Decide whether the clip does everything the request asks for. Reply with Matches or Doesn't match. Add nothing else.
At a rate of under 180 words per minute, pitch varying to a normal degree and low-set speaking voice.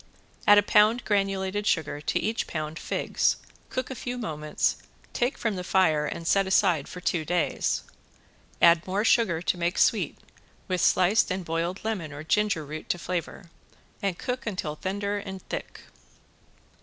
Doesn't match